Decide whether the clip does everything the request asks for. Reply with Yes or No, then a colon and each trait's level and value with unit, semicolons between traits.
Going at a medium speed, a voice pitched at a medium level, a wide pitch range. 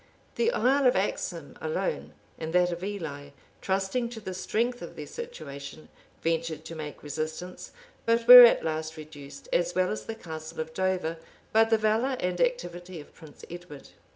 Yes: average, 170 wpm; medium, 180 Hz; wide, 6.4 semitones